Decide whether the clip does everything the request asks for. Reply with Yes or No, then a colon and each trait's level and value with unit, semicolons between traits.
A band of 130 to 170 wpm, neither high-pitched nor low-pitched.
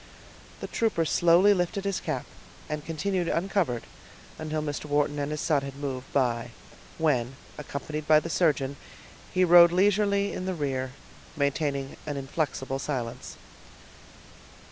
Yes: slow, 135 wpm; medium, 150 Hz